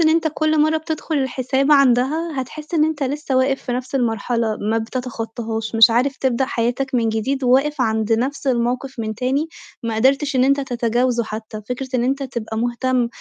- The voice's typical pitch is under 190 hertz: No, very high, 255 Hz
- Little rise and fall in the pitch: No, average, 3.1 semitones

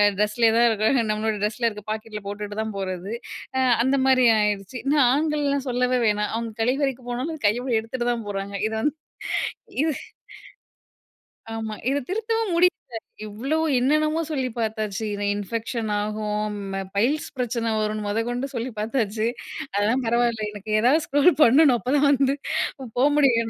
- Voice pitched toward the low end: No, high, 235 Hz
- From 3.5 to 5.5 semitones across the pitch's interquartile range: Yes, average, 4.1 semitones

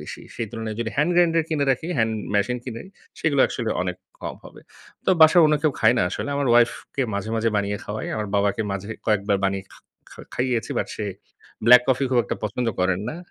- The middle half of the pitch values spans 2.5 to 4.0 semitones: No, average, 4.8 semitones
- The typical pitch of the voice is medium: No, low, 115 Hz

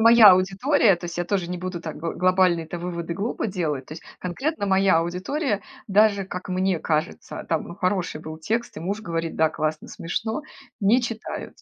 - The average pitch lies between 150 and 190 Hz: Yes, medium, 185 Hz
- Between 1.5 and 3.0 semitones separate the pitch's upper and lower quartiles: No, average, 3.4 semitones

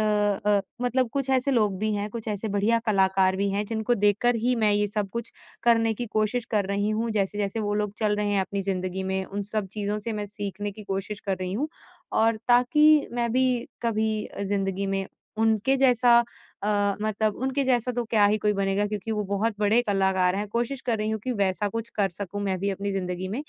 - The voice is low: No, high, 210 Hz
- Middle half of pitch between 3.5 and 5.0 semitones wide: No, narrow, 2.5 semitones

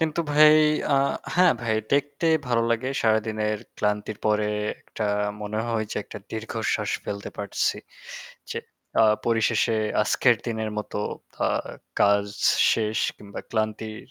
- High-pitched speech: No, low, 110 Hz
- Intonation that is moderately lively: No, narrow, 1.7 semitones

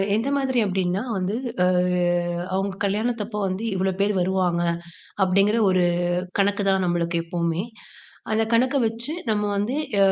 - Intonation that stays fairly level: No, average, 3.2 semitones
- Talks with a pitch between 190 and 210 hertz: Yes, high, 200 Hz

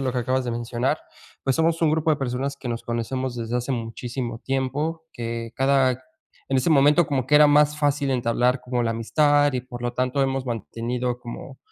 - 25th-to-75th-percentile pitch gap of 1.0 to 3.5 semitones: Yes, average, 2.8 semitones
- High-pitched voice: No, low, 130 Hz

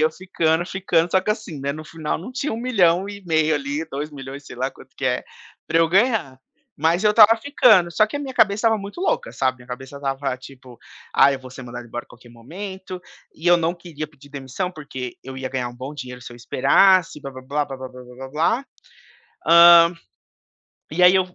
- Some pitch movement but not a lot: No, wide, 6.0 semitones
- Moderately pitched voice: Yes, medium, 155 Hz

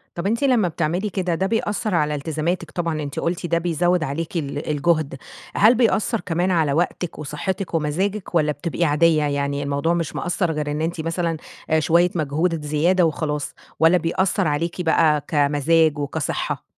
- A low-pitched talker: No, medium, 165 Hz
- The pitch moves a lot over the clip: No, average, 2.9 semitones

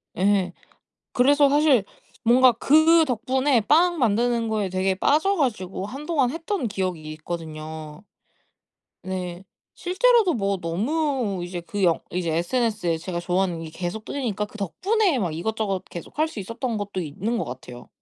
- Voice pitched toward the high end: Yes, high, 210 Hz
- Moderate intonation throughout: No, wide, 7.4 semitones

